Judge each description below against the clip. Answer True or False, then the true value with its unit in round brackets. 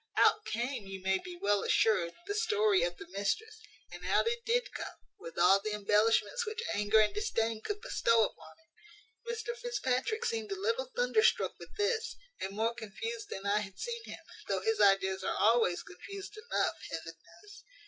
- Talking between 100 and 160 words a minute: False (180 wpm)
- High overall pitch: True (360 Hz)